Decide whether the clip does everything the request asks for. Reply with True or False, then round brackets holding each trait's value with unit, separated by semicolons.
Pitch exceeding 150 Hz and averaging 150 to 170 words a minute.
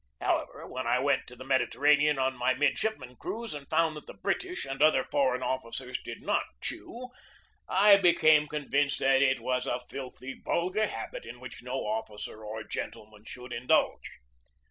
False (135 Hz; 165 wpm)